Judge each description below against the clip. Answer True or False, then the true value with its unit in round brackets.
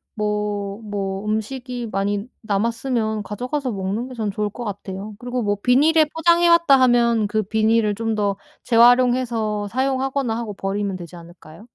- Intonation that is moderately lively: True (3.4 semitones)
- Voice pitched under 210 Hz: False (220 Hz)